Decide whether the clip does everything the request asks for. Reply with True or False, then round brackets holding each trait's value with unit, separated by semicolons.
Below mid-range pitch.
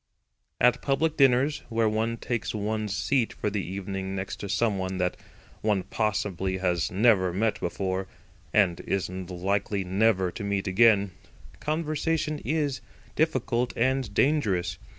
True (105 Hz)